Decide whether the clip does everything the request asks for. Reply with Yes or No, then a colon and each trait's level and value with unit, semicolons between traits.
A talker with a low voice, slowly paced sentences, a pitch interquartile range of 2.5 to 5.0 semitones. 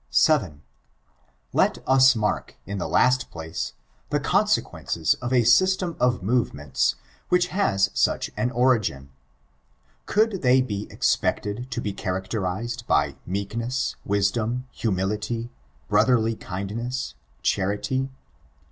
Yes: low, 115 Hz; slow, 110 wpm; average, 4.4 semitones